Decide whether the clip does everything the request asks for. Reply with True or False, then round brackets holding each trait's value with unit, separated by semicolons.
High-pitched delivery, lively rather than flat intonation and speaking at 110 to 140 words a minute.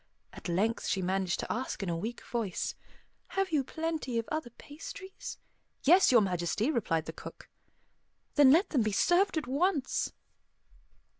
False (250 Hz; 8.2 semitones; 155 wpm)